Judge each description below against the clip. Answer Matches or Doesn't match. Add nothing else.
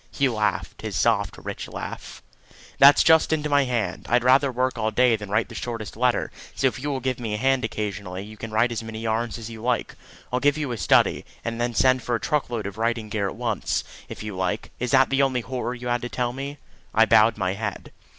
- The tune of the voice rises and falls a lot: Doesn't match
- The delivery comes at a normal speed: Doesn't match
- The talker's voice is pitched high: Doesn't match